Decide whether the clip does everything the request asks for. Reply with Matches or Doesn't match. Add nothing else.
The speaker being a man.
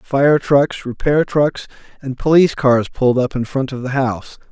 Matches